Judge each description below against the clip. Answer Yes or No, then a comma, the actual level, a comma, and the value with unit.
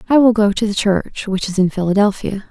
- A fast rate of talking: Yes, fast, 240 wpm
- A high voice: Yes, high, 205 Hz